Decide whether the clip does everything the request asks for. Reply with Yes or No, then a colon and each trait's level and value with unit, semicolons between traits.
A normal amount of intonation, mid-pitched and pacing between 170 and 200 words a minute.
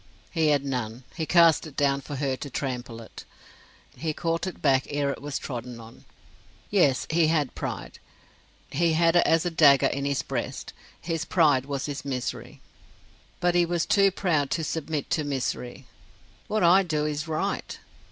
Yes: average, 3.3 semitones; medium, 150 Hz; average, 175 wpm